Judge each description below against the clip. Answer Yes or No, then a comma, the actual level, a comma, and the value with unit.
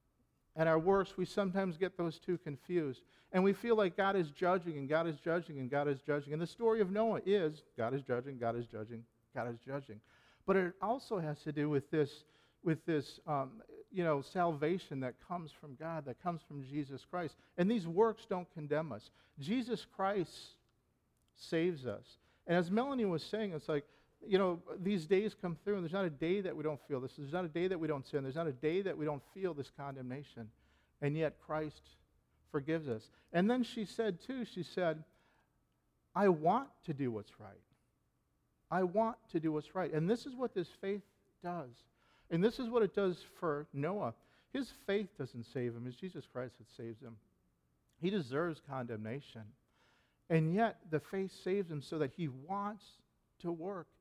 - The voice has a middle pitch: Yes, medium, 160 Hz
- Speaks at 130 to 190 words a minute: No, average, 200 wpm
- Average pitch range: No, wide, 5.7 semitones